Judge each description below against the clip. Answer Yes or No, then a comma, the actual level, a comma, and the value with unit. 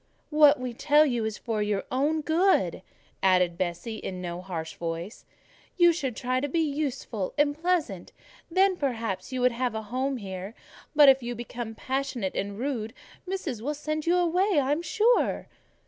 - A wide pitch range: Yes, wide, 6.3 semitones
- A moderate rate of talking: Yes, average, 170 wpm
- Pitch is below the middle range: No, very high, 255 Hz